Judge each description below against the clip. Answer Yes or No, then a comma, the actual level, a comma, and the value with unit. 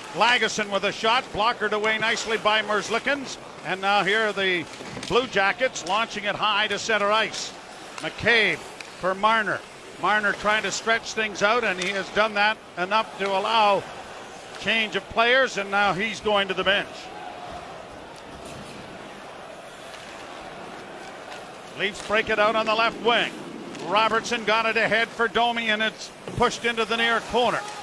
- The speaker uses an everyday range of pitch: No, narrow, 2.2 semitones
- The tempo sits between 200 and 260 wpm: No, average, 150 wpm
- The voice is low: No, high, 215 Hz